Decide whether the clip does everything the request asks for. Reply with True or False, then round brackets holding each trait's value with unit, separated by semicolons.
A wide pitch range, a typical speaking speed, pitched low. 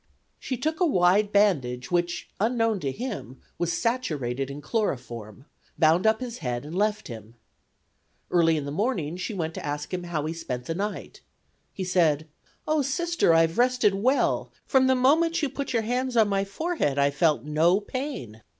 False (8.5 semitones; 180 wpm; 185 Hz)